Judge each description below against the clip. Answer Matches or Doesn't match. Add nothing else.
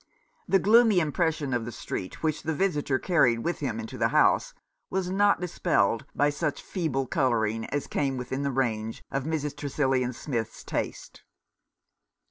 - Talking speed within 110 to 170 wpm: Matches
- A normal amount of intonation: Matches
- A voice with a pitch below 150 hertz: Matches